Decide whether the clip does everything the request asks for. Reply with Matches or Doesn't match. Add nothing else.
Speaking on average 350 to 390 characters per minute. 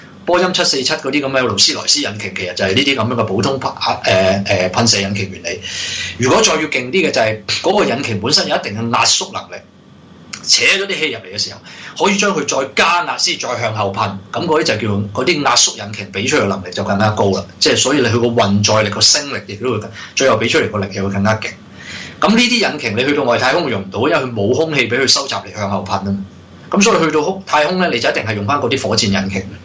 Matches